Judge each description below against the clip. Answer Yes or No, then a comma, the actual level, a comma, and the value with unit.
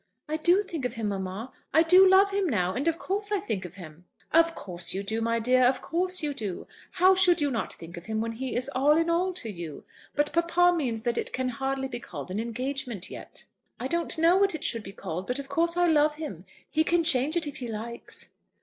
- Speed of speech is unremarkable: No, fast, 245 wpm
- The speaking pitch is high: Yes, very high, 270 Hz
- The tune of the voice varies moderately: No, wide, 7.1 semitones